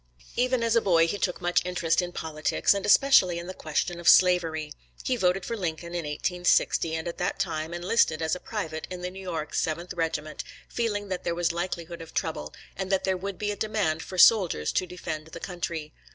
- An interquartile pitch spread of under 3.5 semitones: Yes, average, 2.9 semitones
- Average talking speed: No, fast, 210 wpm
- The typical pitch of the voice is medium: Yes, medium, 175 Hz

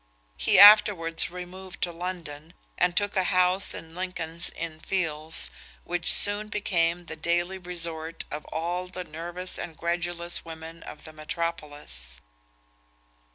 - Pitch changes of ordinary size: No, narrow, 2.1 semitones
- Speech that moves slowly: Yes, slow, 130 wpm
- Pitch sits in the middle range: Yes, medium, 170 Hz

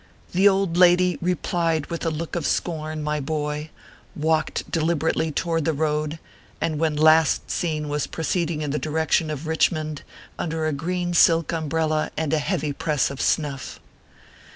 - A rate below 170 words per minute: Yes, average, 155 wpm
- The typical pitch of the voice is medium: Yes, medium, 160 Hz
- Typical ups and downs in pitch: No, narrow, 1.7 semitones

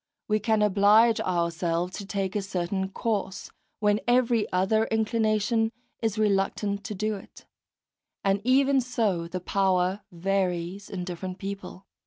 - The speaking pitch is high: Yes, high, 200 Hz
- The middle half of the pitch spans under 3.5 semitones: Yes, average, 2.7 semitones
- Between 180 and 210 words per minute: No, slow, 135 wpm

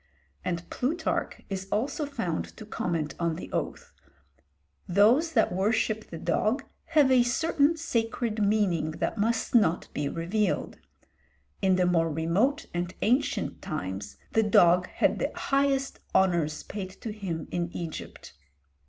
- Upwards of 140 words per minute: No, slow, 135 wpm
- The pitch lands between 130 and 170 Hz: No, high, 205 Hz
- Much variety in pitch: Yes, wide, 6.2 semitones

